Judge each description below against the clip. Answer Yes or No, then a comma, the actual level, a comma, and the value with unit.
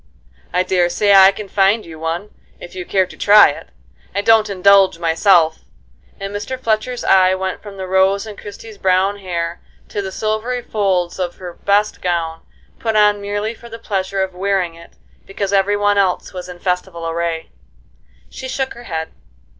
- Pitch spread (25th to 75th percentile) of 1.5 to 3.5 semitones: Yes, narrow, 2.4 semitones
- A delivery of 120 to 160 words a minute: No, average, 180 wpm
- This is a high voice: Yes, high, 195 Hz